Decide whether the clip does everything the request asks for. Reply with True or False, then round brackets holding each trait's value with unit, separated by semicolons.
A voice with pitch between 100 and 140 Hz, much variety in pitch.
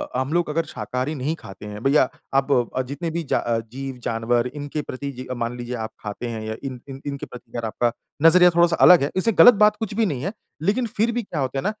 True (135 Hz; 5.7 semitones)